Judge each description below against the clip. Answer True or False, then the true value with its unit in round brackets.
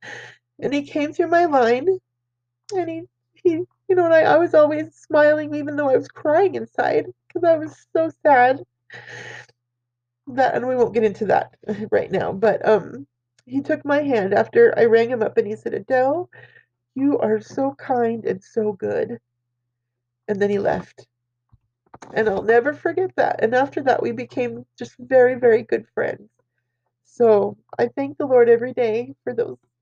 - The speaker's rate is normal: True (175 wpm)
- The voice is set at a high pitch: True (245 Hz)